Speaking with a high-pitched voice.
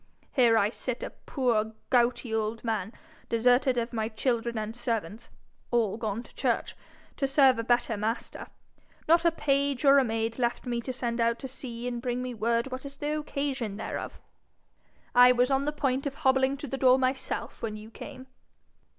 Yes: high, 245 Hz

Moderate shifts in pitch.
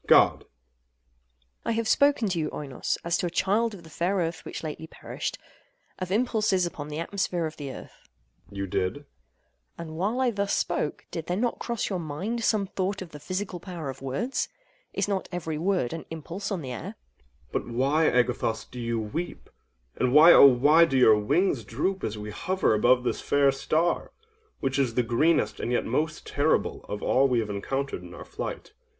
No: wide, 7.1 semitones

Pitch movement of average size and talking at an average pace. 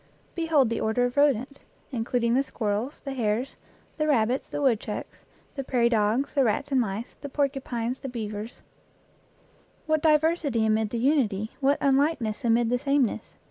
Yes: average, 3.8 semitones; average, 160 wpm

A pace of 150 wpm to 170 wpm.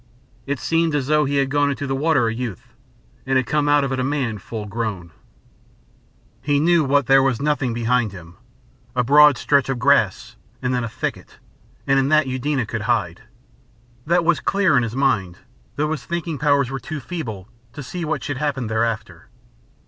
No: average, 185 wpm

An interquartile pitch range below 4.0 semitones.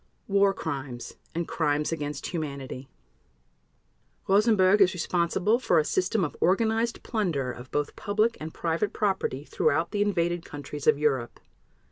No: wide, 5.5 semitones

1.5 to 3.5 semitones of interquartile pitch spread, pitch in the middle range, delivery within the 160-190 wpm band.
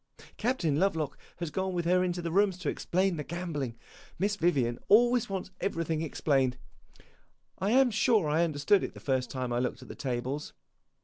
No: average, 5.2 semitones; medium, 170 Hz; average, 180 wpm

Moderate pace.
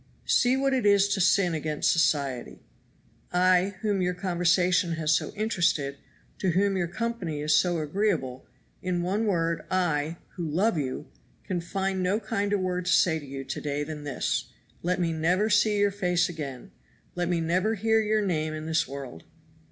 Yes: average, 175 wpm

